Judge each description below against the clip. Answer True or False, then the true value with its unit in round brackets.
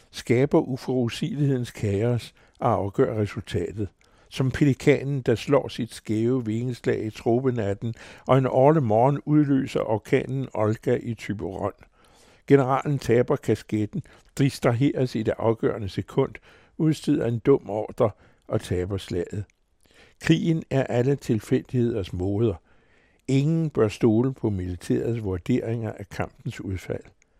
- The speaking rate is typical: False (115 wpm)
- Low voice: True (120 Hz)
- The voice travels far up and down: False (3.9 semitones)